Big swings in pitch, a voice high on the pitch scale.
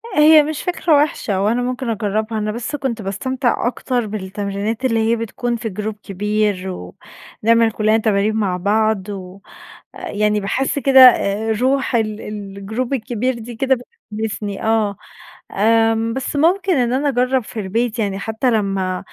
No: average, 3.4 semitones; high, 220 Hz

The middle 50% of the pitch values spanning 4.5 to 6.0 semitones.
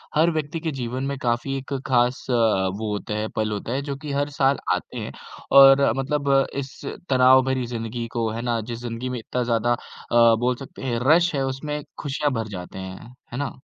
No: average, 3.2 semitones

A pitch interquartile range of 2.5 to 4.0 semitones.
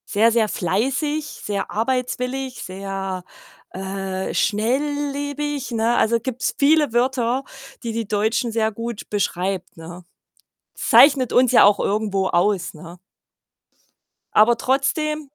No: average, 5.1 semitones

